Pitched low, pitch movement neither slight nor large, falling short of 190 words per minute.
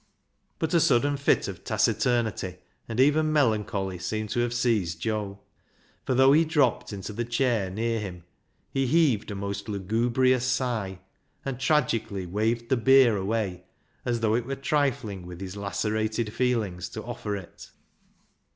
Yes: low, 115 Hz; average, 4.2 semitones; average, 150 wpm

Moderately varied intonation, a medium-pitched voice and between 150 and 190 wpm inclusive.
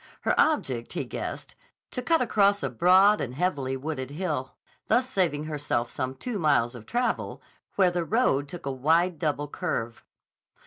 No: wide, 6.5 semitones; medium, 155 Hz; average, 165 wpm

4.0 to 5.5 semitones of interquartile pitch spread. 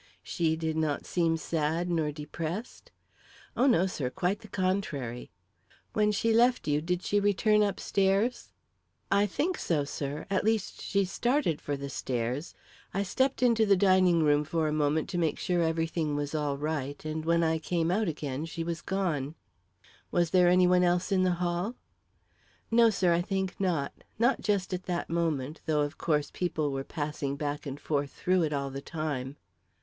Yes: average, 4.3 semitones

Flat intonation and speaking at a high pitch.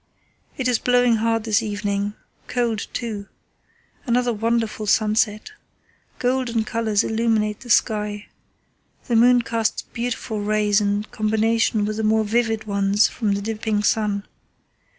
Yes: narrow, 1.7 semitones; high, 220 Hz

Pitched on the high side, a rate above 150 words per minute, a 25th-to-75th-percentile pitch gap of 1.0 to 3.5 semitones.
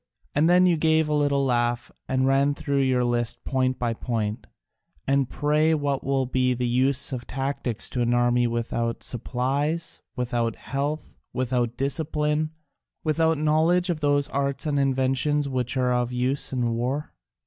No: low, 135 Hz; average, 160 wpm; average, 3.1 semitones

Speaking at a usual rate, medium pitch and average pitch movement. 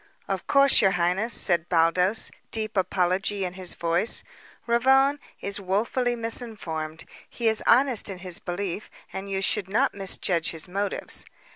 No: average, 145 wpm; high, 195 Hz; average, 4.1 semitones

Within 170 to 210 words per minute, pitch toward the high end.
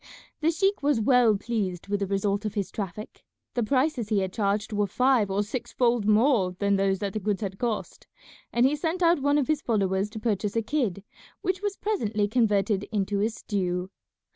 Yes: average, 200 wpm; high, 215 Hz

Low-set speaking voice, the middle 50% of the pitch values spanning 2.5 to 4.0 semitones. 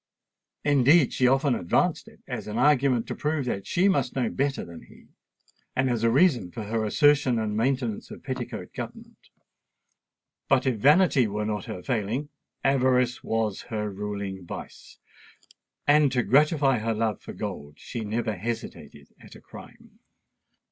No: low, 120 Hz; average, 4.4 semitones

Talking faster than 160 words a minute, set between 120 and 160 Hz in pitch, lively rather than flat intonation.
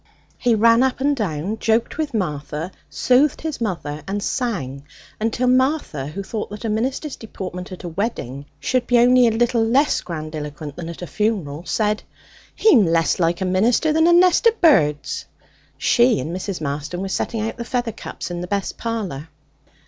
No: average, 180 wpm; high, 210 Hz; wide, 6.6 semitones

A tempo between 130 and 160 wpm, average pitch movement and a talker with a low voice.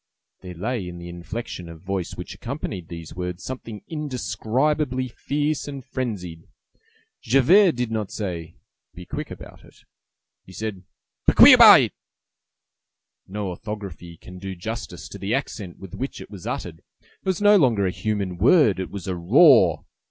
No: average, 150 wpm; wide, 6.3 semitones; low, 105 Hz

